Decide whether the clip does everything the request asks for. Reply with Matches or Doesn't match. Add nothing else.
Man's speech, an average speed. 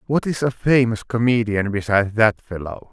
Matches